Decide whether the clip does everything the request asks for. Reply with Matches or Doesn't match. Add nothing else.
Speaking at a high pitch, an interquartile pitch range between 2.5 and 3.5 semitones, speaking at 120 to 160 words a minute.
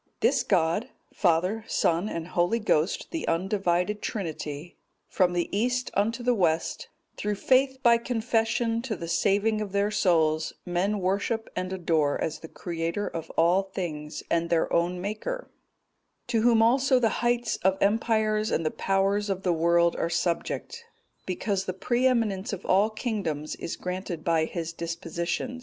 Doesn't match